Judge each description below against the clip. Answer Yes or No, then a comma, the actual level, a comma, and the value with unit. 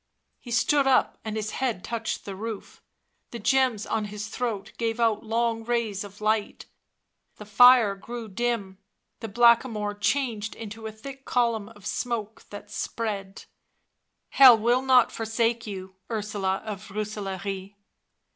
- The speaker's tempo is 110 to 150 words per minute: Yes, average, 145 wpm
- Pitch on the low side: No, high, 220 Hz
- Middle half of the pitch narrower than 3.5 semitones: Yes, narrow, 2.4 semitones